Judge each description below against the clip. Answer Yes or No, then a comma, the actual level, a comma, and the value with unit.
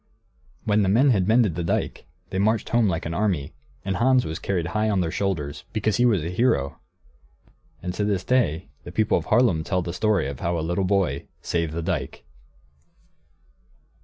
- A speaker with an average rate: Yes, average, 190 wpm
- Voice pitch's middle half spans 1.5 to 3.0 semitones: No, average, 4.5 semitones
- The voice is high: No, very low, 95 Hz